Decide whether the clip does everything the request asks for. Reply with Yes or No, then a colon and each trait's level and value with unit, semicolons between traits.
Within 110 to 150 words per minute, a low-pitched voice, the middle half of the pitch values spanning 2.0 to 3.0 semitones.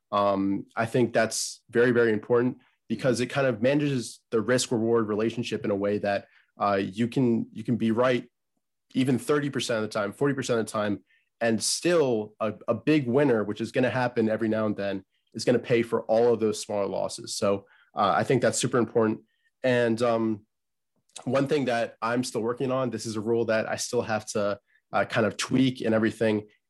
No: fast, 205 wpm; low, 115 Hz; narrow, 2.4 semitones